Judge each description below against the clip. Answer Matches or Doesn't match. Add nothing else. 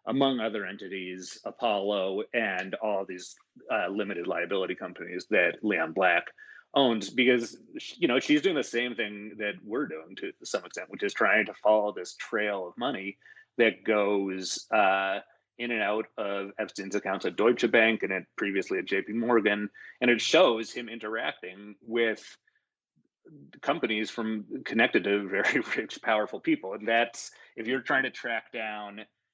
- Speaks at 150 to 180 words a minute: Matches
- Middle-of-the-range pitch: Doesn't match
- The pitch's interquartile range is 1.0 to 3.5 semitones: Matches